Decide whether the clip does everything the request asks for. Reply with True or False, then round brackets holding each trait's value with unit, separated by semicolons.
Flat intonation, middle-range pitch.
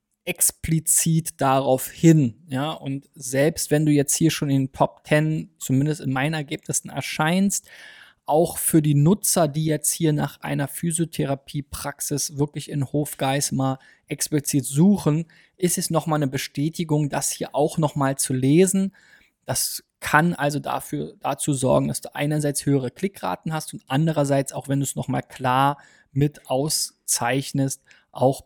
True (2.3 semitones; 150 Hz)